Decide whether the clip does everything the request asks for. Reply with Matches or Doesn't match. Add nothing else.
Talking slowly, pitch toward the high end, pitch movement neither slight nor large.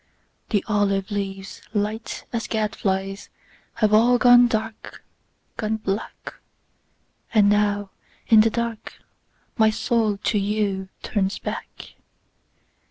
Doesn't match